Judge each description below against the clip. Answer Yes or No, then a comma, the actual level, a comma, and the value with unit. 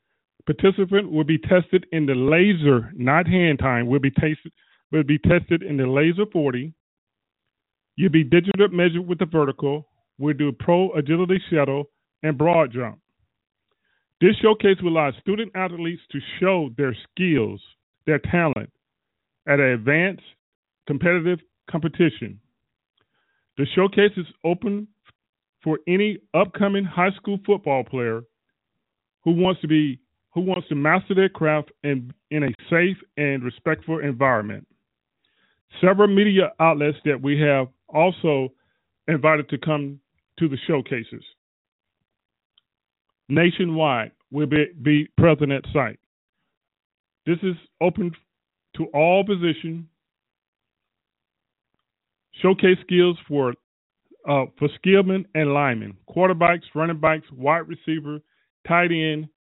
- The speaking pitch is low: No, medium, 160 Hz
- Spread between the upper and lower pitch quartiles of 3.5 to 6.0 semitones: Yes, average, 4.0 semitones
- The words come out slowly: Yes, slow, 120 wpm